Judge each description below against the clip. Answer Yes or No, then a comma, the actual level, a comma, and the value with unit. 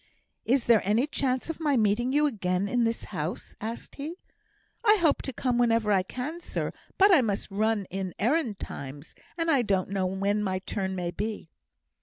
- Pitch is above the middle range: Yes, high, 225 Hz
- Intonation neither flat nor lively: No, wide, 5.7 semitones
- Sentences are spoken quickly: No, average, 190 wpm